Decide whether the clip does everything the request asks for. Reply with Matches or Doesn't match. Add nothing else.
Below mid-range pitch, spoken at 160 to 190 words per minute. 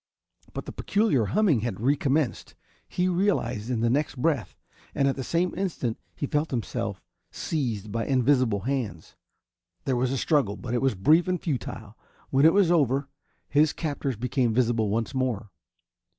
Matches